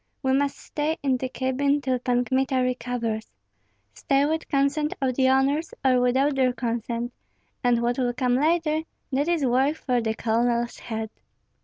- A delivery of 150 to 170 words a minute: Yes, average, 165 wpm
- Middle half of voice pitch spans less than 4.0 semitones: Yes, narrow, 2.5 semitones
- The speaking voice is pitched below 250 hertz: No, very high, 260 Hz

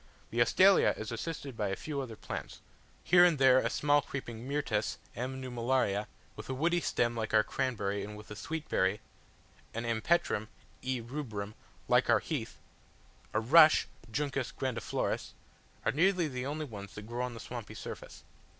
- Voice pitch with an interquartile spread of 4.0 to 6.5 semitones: Yes, average, 4.7 semitones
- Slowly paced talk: No, average, 170 wpm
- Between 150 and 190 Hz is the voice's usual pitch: No, low, 125 Hz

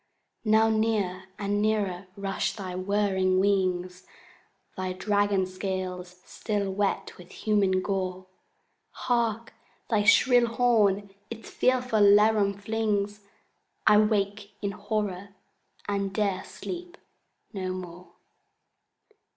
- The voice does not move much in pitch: Yes, narrow, 2.3 semitones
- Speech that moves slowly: Yes, slow, 100 wpm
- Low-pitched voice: No, high, 200 Hz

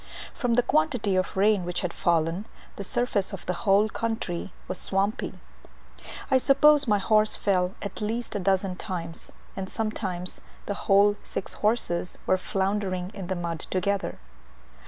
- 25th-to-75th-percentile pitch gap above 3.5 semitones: No, average, 2.8 semitones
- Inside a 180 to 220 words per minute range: No, average, 155 wpm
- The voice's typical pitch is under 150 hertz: No, high, 195 Hz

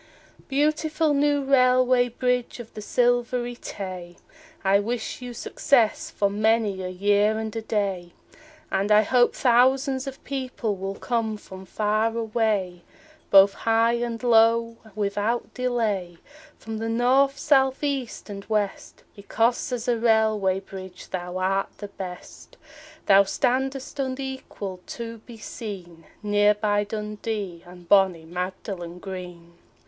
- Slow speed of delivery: Yes, slow, 130 wpm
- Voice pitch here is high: Yes, high, 220 Hz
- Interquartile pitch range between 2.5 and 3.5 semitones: No, average, 3.9 semitones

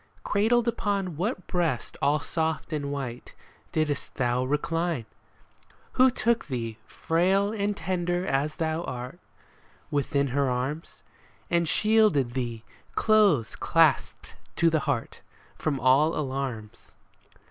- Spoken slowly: Yes, slow, 115 wpm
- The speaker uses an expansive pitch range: Yes, wide, 5.7 semitones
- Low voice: No, medium, 155 Hz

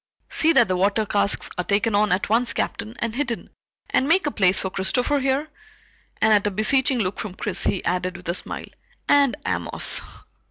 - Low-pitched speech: No, high, 215 Hz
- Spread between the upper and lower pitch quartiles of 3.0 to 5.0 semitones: No, wide, 5.4 semitones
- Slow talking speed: No, average, 195 wpm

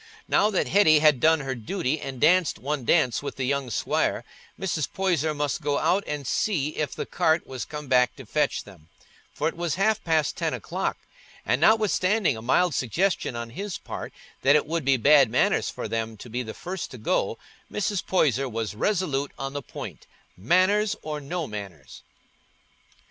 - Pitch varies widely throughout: Yes, wide, 5.7 semitones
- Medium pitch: Yes, medium, 150 Hz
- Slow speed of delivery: No, average, 185 wpm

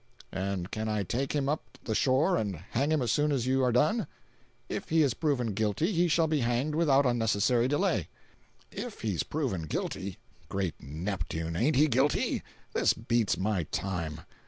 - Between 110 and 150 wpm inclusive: No, average, 175 wpm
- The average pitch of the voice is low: Yes, low, 120 Hz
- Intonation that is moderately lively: No, wide, 6.9 semitones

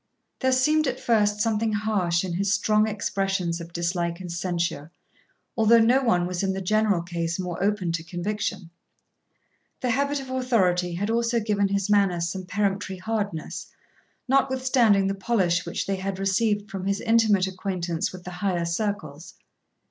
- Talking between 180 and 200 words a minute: No, average, 160 wpm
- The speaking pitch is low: No, high, 195 Hz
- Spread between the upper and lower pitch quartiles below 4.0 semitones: Yes, average, 3.6 semitones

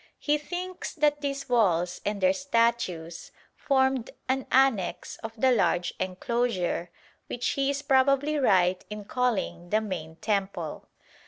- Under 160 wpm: Yes, slow, 135 wpm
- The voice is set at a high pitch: Yes, high, 230 Hz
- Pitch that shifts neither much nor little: No, wide, 6.5 semitones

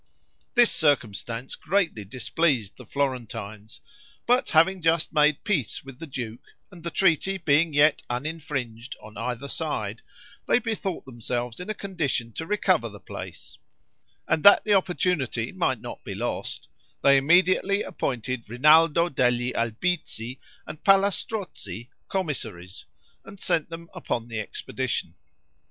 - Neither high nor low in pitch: Yes, medium, 145 Hz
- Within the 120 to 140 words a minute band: Yes, slow, 135 wpm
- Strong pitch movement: Yes, wide, 6.8 semitones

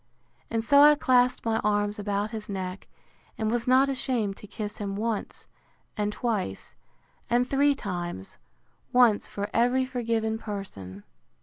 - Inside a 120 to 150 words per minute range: Yes, average, 140 wpm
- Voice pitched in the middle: No, high, 220 Hz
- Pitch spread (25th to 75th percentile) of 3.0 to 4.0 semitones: Yes, average, 3.4 semitones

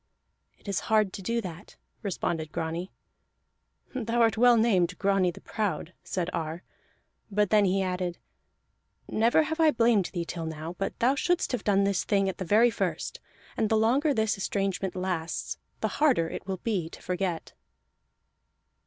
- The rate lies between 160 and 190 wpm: Yes, average, 165 wpm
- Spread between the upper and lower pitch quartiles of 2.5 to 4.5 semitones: Yes, average, 4.1 semitones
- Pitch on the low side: No, high, 195 Hz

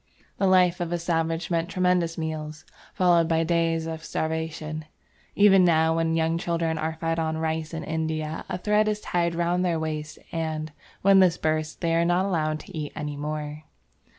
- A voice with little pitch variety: Yes, narrow, 1.6 semitones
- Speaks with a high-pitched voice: No, medium, 165 Hz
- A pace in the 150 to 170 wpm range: No, average, 180 wpm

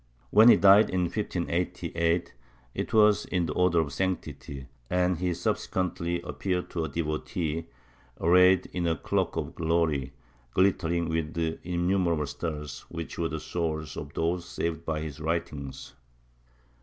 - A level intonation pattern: Yes, narrow, 2.2 semitones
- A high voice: No, very low, 85 Hz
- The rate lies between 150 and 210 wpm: No, average, 140 wpm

